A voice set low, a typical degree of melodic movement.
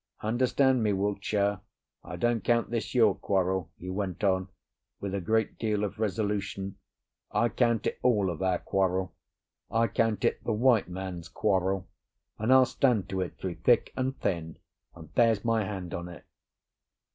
Yes: low, 100 Hz; average, 3.3 semitones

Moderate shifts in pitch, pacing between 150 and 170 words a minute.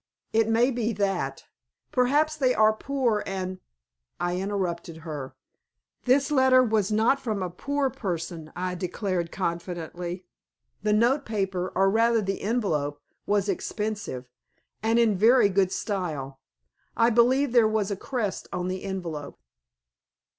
No: average, 4.6 semitones; slow, 135 wpm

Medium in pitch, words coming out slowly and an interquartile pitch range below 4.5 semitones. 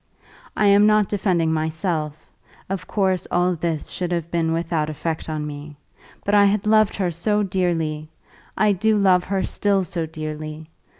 No: medium, 175 Hz; average, 165 wpm; average, 4.0 semitones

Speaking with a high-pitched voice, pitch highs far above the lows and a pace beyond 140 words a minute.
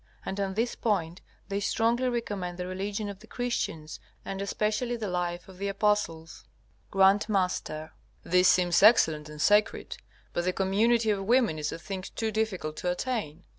No: high, 195 Hz; average, 3.5 semitones; average, 165 wpm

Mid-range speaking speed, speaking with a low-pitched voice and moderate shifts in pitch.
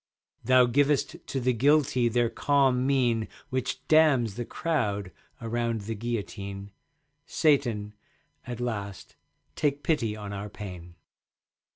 No: slow, 115 wpm; low, 120 Hz; average, 4.3 semitones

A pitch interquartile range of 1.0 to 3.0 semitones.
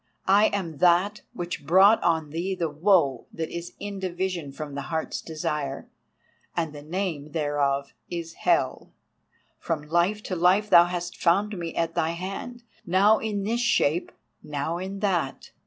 No: average, 3.9 semitones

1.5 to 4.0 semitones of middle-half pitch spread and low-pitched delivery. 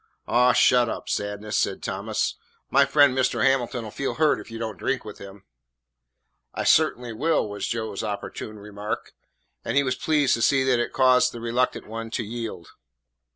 Yes: average, 3.2 semitones; low, 120 Hz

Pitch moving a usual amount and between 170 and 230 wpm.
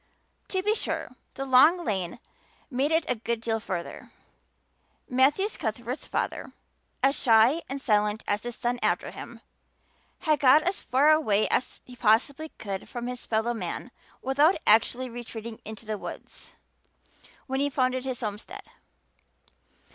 No: average, 4.1 semitones; average, 145 wpm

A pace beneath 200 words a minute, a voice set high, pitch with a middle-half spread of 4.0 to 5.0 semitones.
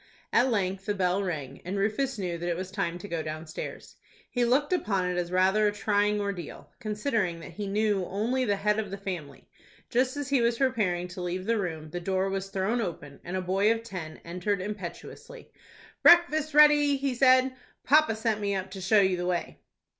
No: fast, 205 wpm; high, 200 Hz; average, 4.3 semitones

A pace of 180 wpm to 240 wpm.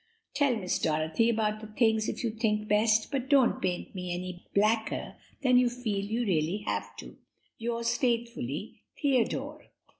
No: average, 155 wpm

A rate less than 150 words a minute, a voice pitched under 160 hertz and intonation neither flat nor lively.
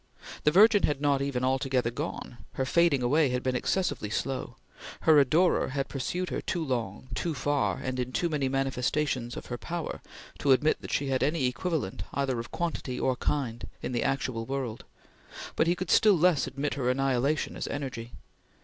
No: average, 185 wpm; low, 135 Hz; average, 3.3 semitones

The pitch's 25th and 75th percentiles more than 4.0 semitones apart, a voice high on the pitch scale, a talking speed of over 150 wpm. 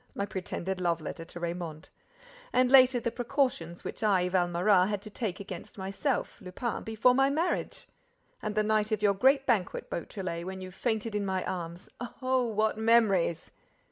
Yes: average, 4.4 semitones; high, 205 Hz; average, 170 wpm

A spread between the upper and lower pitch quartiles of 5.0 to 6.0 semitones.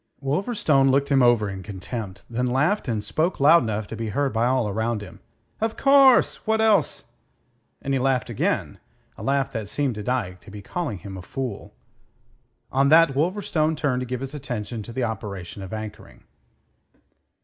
Yes: average, 5.3 semitones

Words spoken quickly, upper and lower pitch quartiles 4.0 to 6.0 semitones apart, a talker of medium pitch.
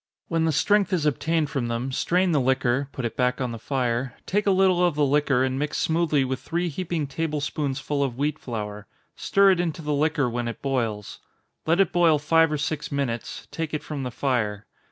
Yes: fast, 215 wpm; average, 4.3 semitones; medium, 145 Hz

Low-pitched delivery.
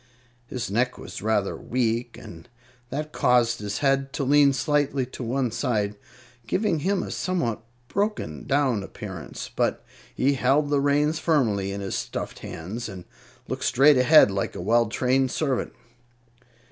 Yes: low, 125 Hz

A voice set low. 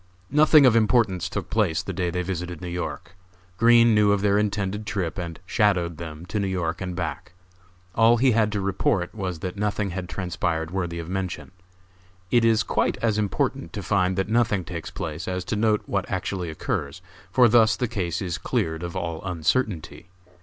Yes: very low, 95 Hz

